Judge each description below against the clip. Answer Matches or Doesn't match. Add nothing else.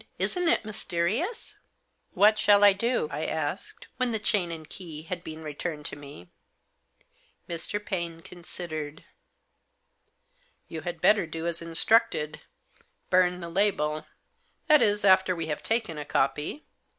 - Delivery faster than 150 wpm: Matches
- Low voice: Doesn't match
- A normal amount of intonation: Matches